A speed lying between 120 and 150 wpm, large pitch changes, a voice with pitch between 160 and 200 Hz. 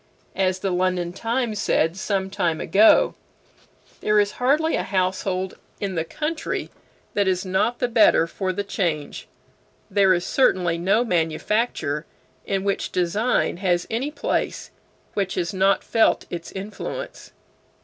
No: average, 140 wpm; average, 3.1 semitones; high, 190 Hz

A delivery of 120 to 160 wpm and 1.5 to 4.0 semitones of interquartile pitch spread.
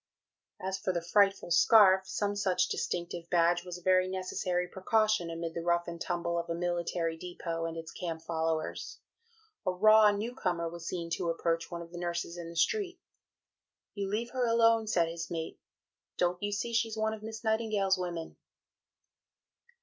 No: average, 180 wpm; average, 3.4 semitones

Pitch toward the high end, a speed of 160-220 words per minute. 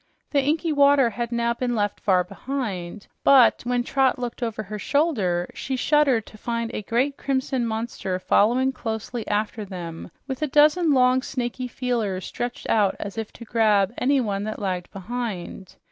Yes: high, 235 Hz; average, 165 wpm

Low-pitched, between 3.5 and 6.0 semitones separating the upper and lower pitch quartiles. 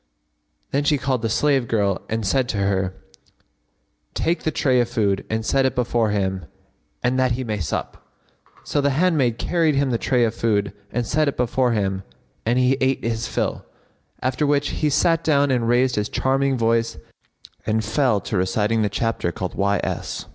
Yes: low, 120 Hz; average, 4.0 semitones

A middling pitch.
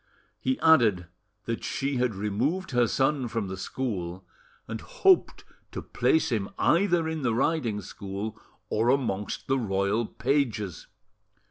No: low, 115 Hz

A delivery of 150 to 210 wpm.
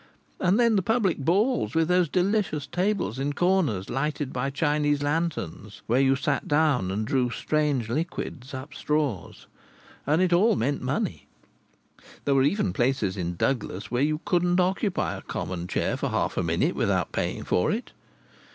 Yes: average, 165 wpm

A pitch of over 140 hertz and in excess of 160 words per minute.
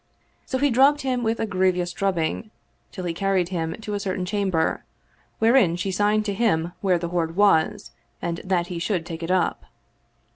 Yes: medium, 185 Hz; average, 190 wpm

